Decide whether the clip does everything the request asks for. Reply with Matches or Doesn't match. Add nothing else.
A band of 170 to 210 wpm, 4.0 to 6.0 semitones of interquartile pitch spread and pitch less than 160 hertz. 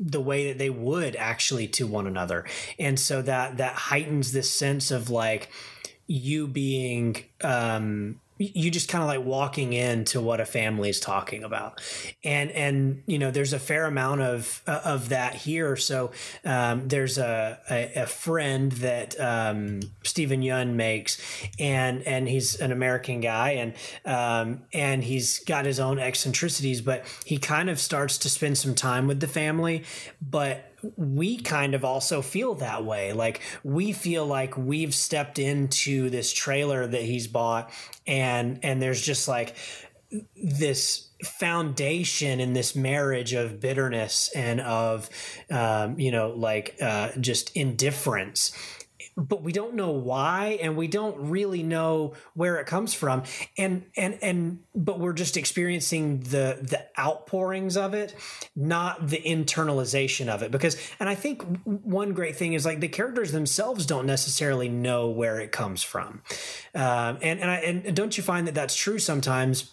Doesn't match